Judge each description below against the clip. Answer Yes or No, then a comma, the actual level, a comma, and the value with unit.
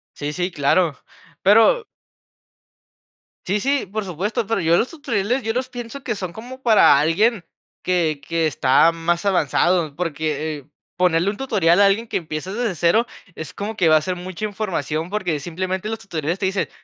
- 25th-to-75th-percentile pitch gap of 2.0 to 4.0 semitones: No, average, 4.8 semitones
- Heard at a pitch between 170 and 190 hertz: Yes, medium, 185 Hz